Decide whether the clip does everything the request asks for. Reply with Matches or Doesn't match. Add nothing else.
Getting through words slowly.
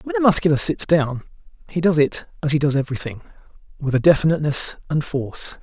Doesn't match